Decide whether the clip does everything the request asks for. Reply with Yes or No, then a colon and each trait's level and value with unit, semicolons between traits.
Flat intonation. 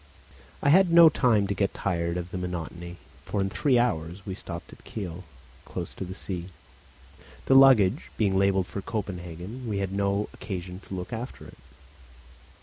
No: average, 3.4 semitones